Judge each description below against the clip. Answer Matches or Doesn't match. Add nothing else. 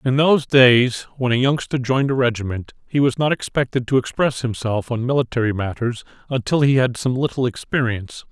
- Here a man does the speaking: Matches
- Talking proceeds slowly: Doesn't match